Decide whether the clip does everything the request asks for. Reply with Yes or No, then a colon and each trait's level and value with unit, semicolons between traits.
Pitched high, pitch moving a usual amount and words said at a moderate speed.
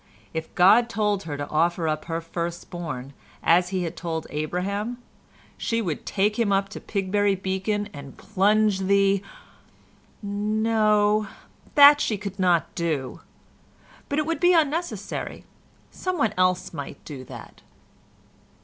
No: high, 195 Hz; average, 4.0 semitones; slow, 130 wpm